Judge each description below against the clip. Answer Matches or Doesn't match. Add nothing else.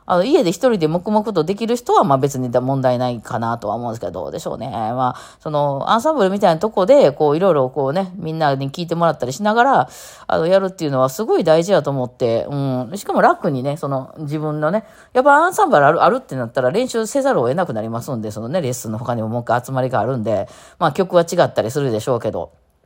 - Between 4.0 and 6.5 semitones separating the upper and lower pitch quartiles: Doesn't match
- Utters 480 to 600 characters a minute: Matches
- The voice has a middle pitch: Matches